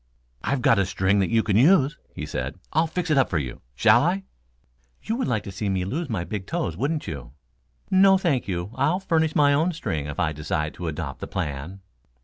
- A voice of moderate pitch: No, low, 110 Hz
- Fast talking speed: Yes, fast, 220 wpm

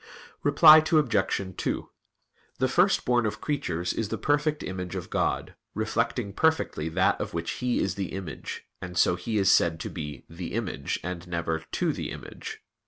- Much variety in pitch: Yes, wide, 6.5 semitones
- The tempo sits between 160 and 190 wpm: Yes, average, 170 wpm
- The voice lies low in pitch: Yes, very low, 95 Hz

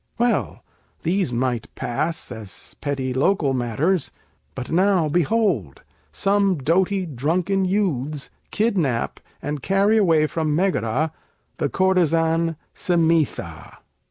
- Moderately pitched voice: Yes, medium, 165 Hz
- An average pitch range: No, wide, 6.1 semitones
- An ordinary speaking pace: No, slow, 100 wpm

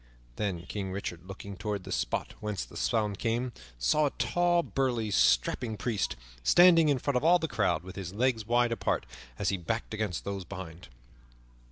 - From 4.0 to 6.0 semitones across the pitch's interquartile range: Yes, average, 4.8 semitones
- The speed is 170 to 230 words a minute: Yes, average, 180 wpm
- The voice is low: Yes, low, 105 Hz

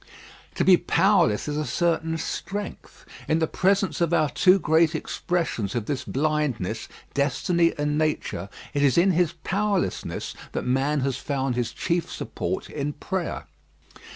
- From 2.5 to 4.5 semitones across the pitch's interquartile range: Yes, average, 4.0 semitones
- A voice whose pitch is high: No, medium, 155 Hz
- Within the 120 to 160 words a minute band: Yes, average, 150 wpm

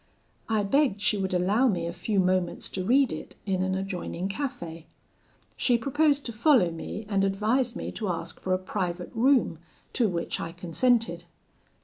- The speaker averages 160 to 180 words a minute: Yes, average, 170 wpm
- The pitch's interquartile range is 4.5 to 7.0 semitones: Yes, average, 5.0 semitones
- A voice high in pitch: Yes, high, 195 Hz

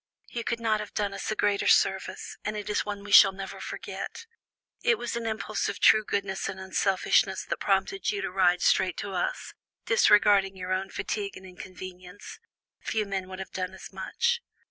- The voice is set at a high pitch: Yes, high, 200 Hz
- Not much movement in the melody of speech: Yes, narrow, 2.2 semitones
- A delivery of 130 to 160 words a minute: No, average, 190 wpm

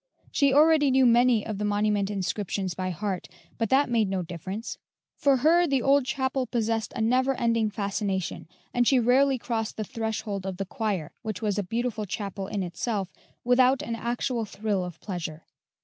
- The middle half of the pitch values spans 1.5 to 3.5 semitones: No, average, 4.1 semitones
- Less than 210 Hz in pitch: No, high, 220 Hz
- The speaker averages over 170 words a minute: Yes, average, 180 wpm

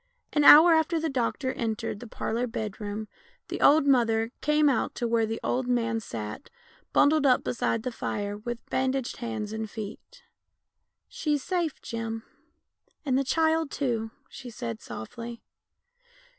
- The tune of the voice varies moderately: Yes, average, 4.2 semitones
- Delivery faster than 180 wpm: No, average, 155 wpm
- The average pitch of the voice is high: Yes, high, 240 Hz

